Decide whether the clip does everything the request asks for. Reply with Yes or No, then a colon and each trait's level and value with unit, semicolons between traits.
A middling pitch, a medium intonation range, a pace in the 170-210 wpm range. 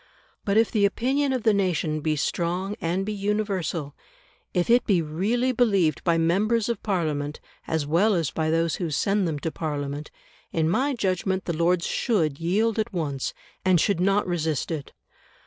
Yes: medium, 180 Hz; average, 4.6 semitones; average, 175 wpm